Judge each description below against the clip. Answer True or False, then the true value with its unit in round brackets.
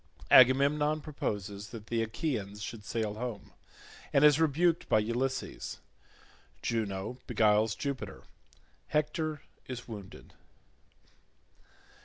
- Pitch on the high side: False (120 Hz)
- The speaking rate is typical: False (85 wpm)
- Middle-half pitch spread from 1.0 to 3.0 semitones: False (5.4 semitones)